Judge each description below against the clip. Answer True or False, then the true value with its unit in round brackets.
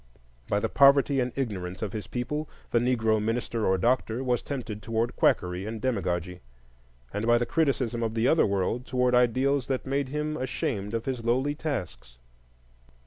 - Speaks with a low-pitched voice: True (120 Hz)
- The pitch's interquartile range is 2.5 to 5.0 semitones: True (3.7 semitones)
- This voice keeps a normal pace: True (170 wpm)